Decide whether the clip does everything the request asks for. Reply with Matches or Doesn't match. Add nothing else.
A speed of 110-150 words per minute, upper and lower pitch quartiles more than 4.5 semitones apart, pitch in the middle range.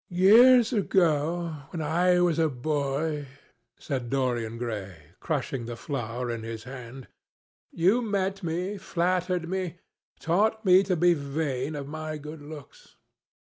Matches